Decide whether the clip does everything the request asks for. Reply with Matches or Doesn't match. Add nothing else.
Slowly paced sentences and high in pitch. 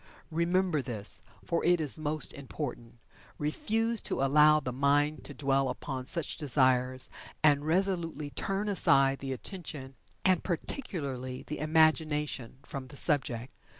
Doesn't match